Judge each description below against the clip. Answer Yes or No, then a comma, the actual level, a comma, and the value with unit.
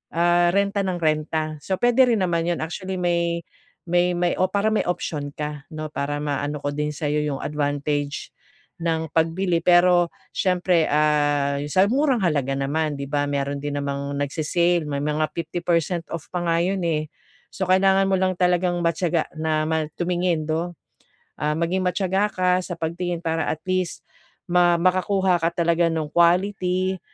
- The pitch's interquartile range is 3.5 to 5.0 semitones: No, average, 3.1 semitones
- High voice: No, medium, 170 Hz